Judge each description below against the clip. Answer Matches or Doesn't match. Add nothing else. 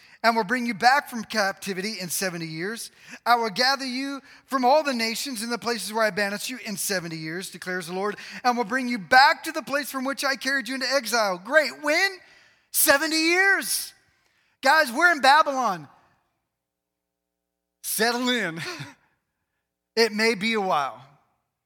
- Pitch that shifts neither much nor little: Doesn't match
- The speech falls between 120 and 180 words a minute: Matches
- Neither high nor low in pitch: Doesn't match